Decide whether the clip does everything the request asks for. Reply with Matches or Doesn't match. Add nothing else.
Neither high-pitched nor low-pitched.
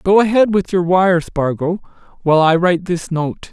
Matches